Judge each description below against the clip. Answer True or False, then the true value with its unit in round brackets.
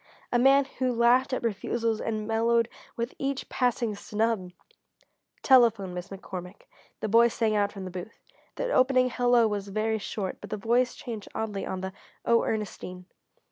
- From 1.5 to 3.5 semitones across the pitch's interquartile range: True (3.2 semitones)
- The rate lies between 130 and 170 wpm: True (165 wpm)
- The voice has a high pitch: True (225 Hz)